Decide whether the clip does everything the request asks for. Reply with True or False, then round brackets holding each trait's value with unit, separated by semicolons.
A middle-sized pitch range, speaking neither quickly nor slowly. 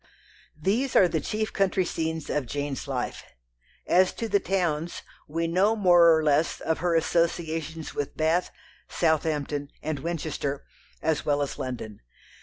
True (3.2 semitones; 145 wpm)